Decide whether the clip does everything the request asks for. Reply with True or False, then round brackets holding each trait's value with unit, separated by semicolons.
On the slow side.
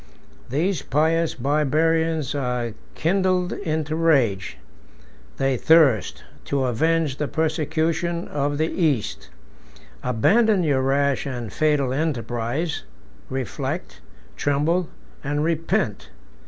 True (95 wpm)